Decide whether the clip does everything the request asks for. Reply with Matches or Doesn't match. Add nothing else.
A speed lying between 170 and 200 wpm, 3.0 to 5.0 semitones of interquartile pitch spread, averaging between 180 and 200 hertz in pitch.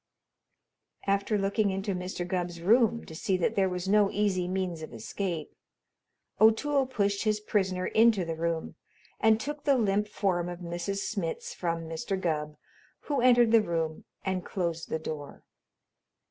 Doesn't match